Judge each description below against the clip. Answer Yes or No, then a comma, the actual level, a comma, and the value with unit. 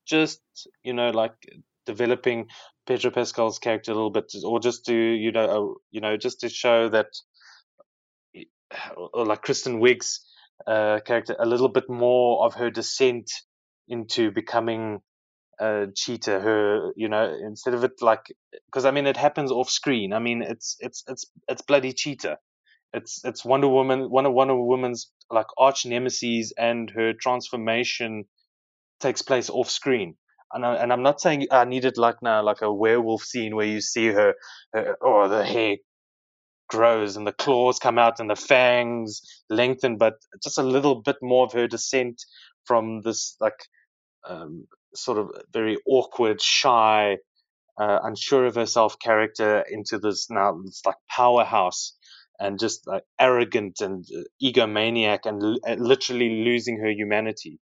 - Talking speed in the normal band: Yes, average, 160 wpm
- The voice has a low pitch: Yes, low, 120 Hz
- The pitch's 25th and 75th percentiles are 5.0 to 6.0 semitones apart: No, average, 2.8 semitones